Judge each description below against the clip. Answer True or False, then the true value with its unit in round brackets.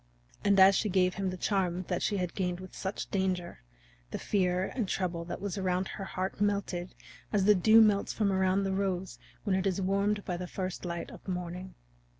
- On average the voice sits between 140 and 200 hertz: True (190 Hz)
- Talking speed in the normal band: False (210 wpm)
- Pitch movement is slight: True (1.6 semitones)